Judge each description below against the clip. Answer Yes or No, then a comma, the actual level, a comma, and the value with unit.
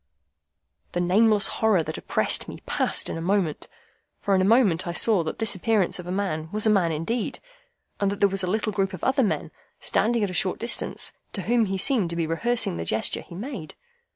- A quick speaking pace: Yes, fast, 220 wpm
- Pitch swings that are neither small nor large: Yes, average, 4.0 semitones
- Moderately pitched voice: No, high, 195 Hz